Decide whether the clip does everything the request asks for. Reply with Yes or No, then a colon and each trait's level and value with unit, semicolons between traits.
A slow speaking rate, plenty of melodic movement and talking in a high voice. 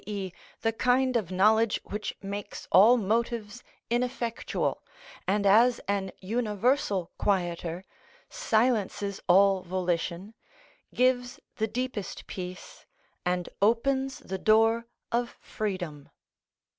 No: slow, 100 wpm; average, 3.9 semitones; high, 210 Hz